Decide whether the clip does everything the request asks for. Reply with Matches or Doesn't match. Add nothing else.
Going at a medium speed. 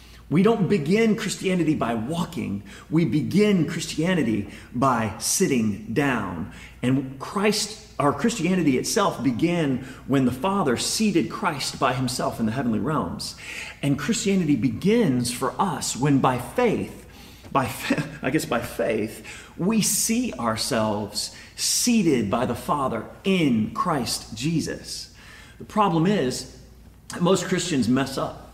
Doesn't match